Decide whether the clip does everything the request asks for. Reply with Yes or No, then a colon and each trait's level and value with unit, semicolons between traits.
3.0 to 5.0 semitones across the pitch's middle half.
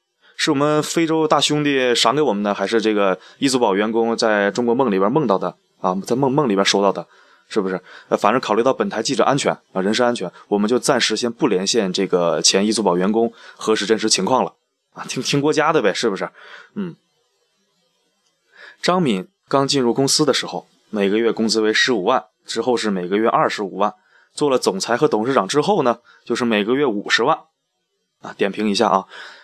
No: wide, 5.4 semitones